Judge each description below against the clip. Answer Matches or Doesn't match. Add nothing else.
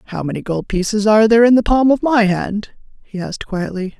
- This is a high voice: Matches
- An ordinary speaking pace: Doesn't match